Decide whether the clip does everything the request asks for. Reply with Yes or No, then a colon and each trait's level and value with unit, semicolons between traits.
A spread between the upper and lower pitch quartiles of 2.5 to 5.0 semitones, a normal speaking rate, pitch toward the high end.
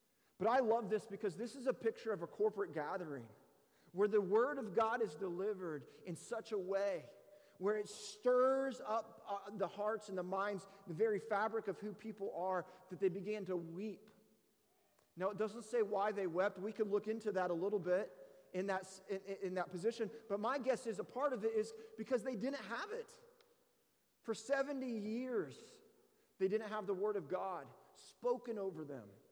Yes: average, 3.2 semitones; average, 190 wpm; high, 210 Hz